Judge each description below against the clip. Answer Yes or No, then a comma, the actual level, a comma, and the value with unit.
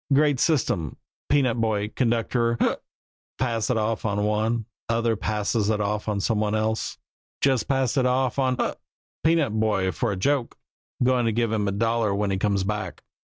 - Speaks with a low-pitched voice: Yes, low, 110 Hz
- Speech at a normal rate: Yes, average, 180 wpm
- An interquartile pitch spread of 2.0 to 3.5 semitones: Yes, average, 3.1 semitones